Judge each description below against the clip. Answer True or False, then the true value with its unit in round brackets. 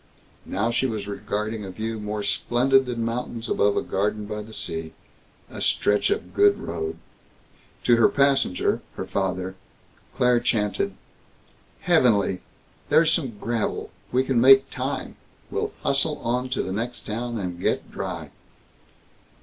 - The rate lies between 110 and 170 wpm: True (140 wpm)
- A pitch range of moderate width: True (3.5 semitones)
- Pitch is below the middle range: True (115 Hz)